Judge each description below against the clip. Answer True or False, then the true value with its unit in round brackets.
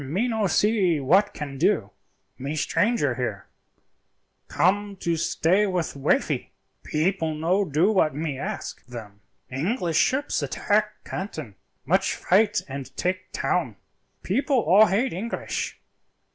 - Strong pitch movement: True (6.0 semitones)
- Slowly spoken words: True (125 wpm)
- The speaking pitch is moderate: True (180 Hz)